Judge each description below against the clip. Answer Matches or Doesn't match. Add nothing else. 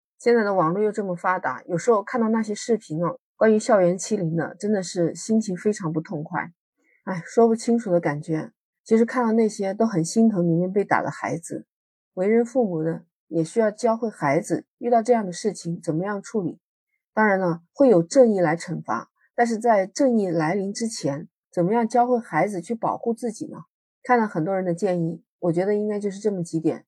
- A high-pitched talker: Matches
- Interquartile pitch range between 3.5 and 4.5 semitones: Doesn't match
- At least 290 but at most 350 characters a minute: Matches